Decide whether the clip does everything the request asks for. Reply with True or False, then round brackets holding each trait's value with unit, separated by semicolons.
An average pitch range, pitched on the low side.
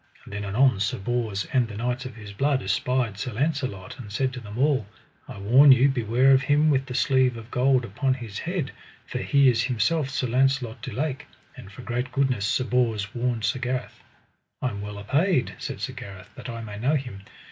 True (3.7 semitones; 125 Hz)